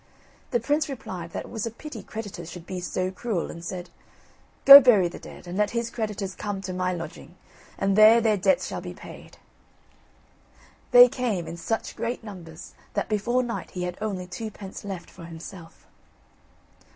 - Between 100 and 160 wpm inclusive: No, average, 175 wpm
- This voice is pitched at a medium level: No, high, 195 Hz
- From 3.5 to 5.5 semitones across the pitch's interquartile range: Yes, average, 4.3 semitones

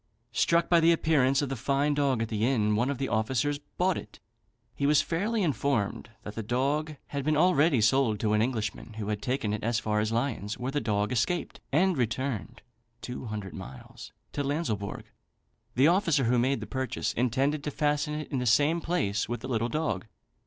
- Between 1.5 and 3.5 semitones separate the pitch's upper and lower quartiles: No, average, 5.0 semitones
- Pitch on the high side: No, low, 130 Hz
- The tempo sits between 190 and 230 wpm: Yes, average, 200 wpm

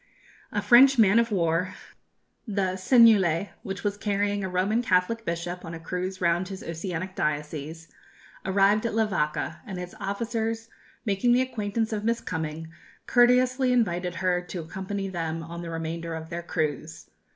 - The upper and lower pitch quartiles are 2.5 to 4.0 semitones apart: No, average, 4.4 semitones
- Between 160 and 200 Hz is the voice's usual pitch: Yes, high, 190 Hz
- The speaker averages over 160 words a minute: No, average, 155 wpm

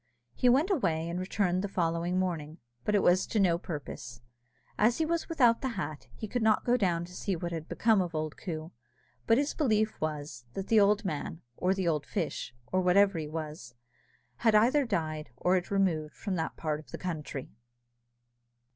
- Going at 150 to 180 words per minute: No, average, 195 wpm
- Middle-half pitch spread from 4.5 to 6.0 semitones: Yes, average, 5.1 semitones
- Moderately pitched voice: Yes, medium, 180 Hz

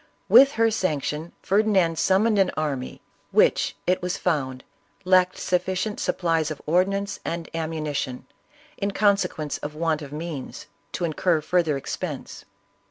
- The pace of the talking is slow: Yes, slow, 130 wpm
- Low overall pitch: No, medium, 170 Hz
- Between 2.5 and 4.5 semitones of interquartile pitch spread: Yes, average, 3.7 semitones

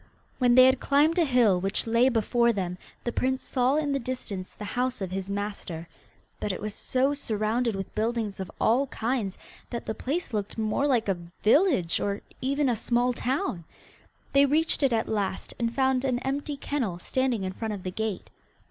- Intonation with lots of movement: No, average, 4.4 semitones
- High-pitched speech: Yes, high, 235 Hz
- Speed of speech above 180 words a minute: Yes, average, 190 wpm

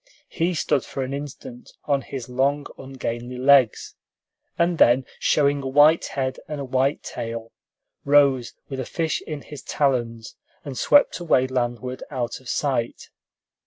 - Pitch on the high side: No, low, 135 Hz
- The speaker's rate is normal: Yes, average, 150 wpm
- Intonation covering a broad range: No, narrow, 2.5 semitones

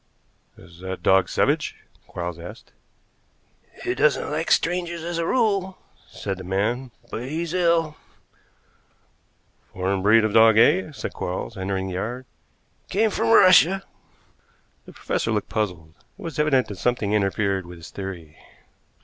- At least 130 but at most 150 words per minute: Yes, average, 140 wpm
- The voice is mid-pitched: No, low, 110 Hz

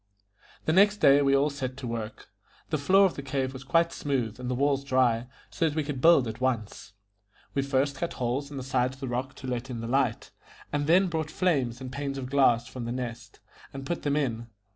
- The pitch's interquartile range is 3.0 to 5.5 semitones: No, narrow, 2.6 semitones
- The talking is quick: Yes, fast, 230 wpm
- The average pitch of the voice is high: No, low, 135 Hz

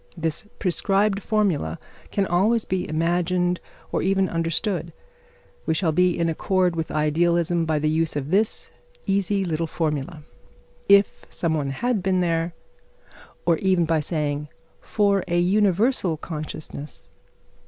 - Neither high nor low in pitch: Yes, medium, 175 Hz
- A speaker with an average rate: No, slow, 130 wpm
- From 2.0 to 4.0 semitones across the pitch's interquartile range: Yes, average, 3.3 semitones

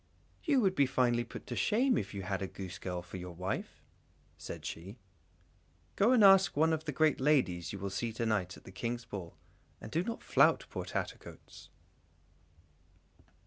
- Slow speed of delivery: No, average, 180 wpm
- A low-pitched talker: Yes, low, 120 Hz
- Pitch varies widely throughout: Yes, wide, 8.9 semitones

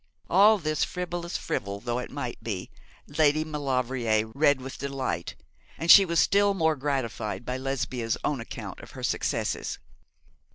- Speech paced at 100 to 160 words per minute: Yes, average, 150 wpm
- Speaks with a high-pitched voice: No, low, 135 Hz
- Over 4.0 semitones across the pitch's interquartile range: Yes, average, 4.8 semitones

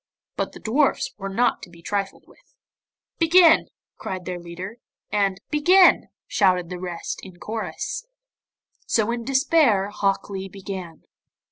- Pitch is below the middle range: No, high, 200 Hz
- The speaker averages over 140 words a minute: No, slow, 135 wpm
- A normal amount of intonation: No, wide, 5.9 semitones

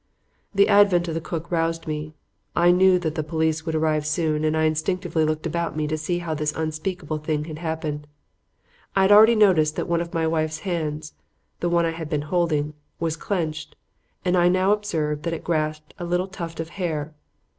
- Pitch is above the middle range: No, medium, 160 Hz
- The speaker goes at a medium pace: No, fast, 210 wpm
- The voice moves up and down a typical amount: No, narrow, 2.2 semitones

